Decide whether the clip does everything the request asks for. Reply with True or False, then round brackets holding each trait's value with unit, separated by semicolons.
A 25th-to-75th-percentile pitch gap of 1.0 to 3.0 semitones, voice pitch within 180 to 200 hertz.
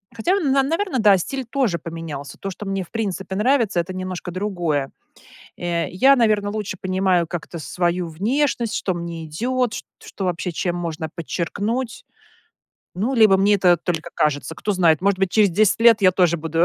False (4.3 semitones; 190 Hz)